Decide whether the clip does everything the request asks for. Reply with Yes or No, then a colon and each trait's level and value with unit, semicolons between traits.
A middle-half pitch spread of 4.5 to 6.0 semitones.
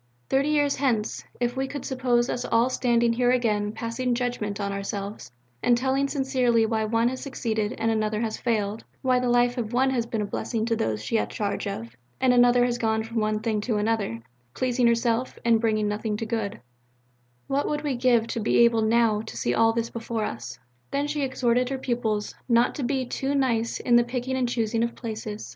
No: narrow, 2.4 semitones